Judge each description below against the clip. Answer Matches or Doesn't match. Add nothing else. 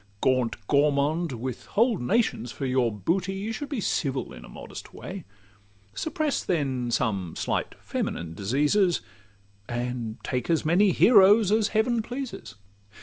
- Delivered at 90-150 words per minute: Matches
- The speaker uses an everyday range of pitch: Doesn't match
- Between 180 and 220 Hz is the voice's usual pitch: Doesn't match